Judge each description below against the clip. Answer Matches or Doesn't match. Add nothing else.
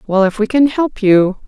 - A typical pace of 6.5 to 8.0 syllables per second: Doesn't match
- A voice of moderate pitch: Doesn't match